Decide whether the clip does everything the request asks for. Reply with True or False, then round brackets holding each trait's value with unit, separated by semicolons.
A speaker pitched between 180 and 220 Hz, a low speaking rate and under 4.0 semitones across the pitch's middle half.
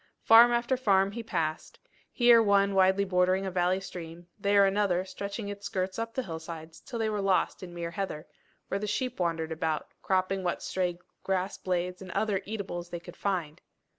False (190 Hz; 185 wpm; 2.6 semitones)